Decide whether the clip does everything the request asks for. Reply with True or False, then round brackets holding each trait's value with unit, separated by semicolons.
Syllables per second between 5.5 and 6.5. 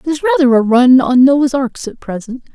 False (5.0 syllables/s)